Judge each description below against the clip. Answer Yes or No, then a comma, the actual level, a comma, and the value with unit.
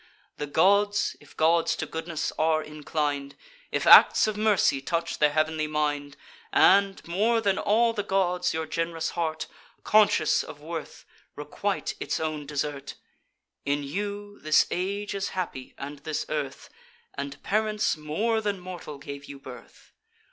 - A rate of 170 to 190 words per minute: No, average, 145 wpm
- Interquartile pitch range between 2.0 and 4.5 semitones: No, average, 5.1 semitones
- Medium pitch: Yes, medium, 160 Hz